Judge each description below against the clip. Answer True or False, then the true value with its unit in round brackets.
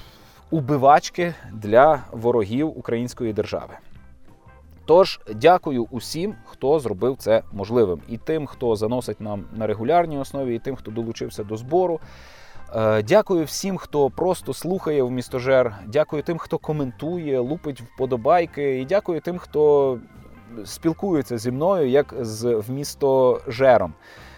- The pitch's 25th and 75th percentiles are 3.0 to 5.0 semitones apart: False (5.5 semitones)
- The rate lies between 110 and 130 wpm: True (120 wpm)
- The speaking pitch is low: True (130 Hz)